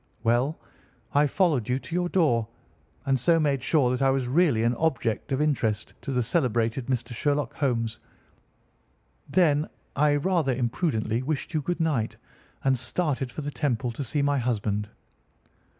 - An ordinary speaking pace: Yes, average, 160 wpm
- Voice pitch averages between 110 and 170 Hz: Yes, low, 135 Hz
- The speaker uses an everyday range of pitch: Yes, average, 4.2 semitones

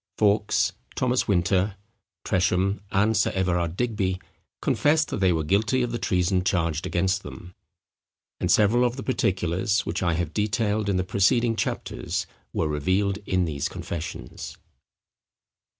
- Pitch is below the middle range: Yes, very low, 95 Hz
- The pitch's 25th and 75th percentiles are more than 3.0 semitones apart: Yes, average, 3.5 semitones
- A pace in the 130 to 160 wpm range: Yes, average, 140 wpm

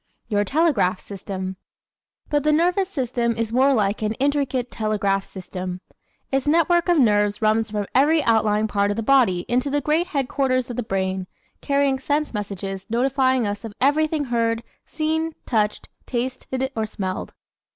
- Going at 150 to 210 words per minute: Yes, average, 160 wpm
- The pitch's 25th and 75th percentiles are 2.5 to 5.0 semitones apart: No, wide, 5.4 semitones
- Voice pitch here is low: No, high, 240 Hz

